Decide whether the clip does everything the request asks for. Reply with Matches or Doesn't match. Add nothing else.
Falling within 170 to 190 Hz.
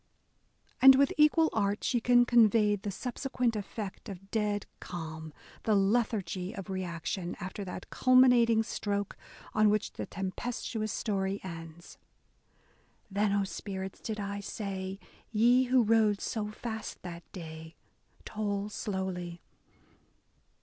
Doesn't match